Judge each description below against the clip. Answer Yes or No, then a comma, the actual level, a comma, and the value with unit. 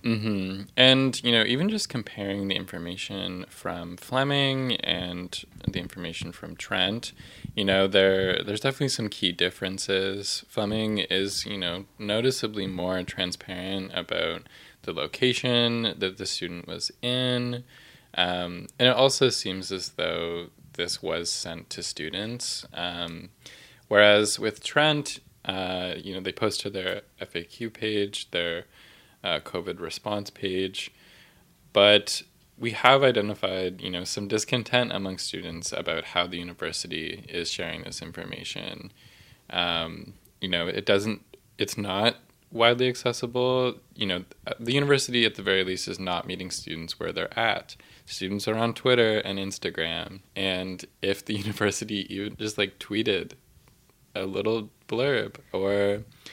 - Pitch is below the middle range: Yes, low, 100 Hz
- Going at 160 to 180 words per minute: No, average, 140 wpm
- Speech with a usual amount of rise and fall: Yes, average, 4.1 semitones